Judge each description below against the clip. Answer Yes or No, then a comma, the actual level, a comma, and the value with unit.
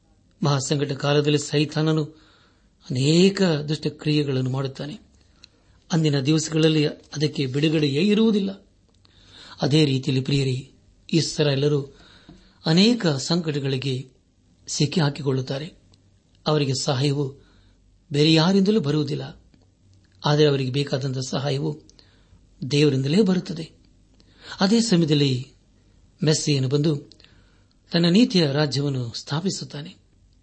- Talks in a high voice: No, medium, 145 Hz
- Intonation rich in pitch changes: Yes, wide, 7.7 semitones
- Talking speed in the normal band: Yes, average, 75 wpm